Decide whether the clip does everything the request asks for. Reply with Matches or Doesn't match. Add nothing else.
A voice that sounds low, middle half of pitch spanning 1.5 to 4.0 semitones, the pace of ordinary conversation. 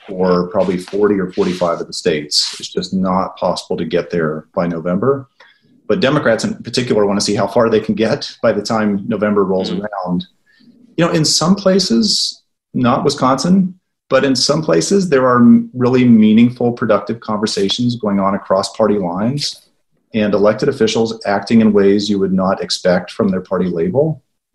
Doesn't match